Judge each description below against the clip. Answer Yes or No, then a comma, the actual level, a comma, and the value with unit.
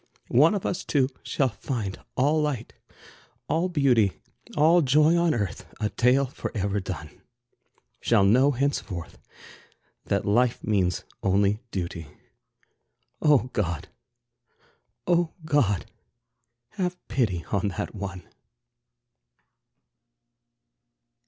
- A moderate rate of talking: No, slow, 100 wpm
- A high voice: No, low, 120 Hz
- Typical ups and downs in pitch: No, wide, 7.1 semitones